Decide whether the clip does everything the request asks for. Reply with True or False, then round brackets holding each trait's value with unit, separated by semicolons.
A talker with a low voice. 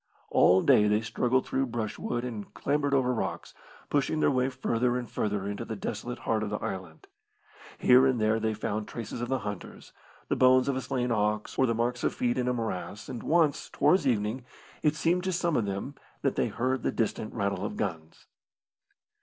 True (120 Hz)